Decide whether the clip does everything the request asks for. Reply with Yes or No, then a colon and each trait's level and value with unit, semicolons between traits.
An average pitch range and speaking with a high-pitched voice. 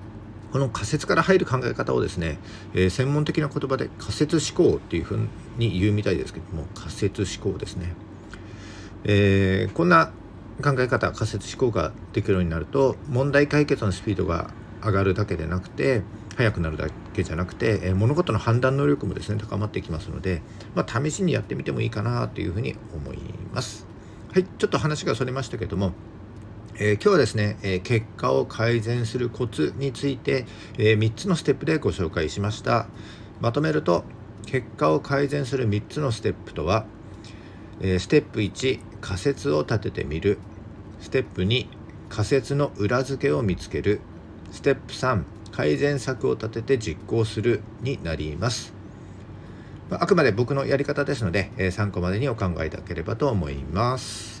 No: average, 4.7 semitones; low, 110 Hz